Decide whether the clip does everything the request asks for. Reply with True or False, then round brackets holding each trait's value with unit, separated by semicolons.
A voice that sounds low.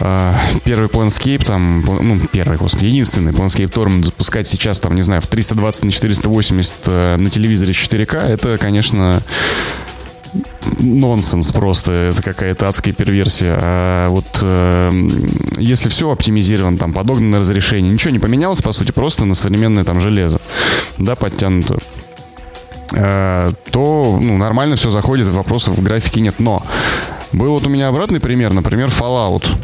True (105 Hz)